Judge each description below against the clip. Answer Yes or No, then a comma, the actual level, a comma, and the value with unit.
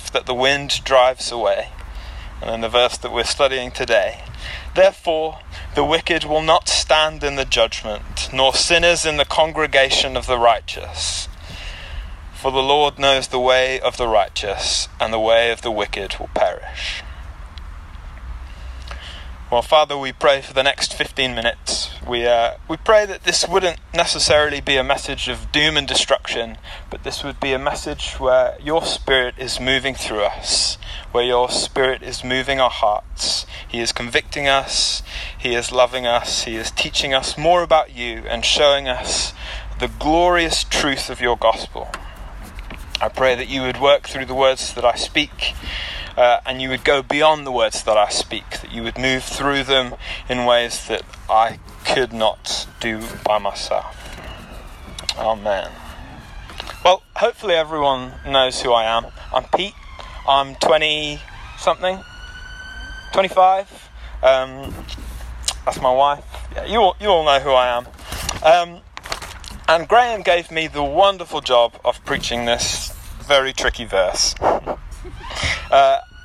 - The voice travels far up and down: No, average, 4.7 semitones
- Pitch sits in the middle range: No, low, 130 Hz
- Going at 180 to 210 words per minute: No, average, 155 wpm